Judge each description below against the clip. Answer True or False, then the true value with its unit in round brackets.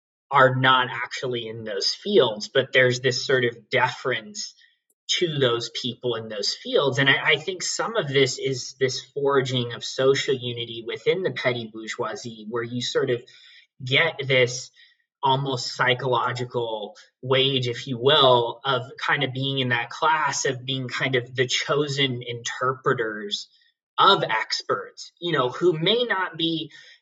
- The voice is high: False (130 Hz)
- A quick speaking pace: False (155 wpm)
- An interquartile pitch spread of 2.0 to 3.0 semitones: False (4.2 semitones)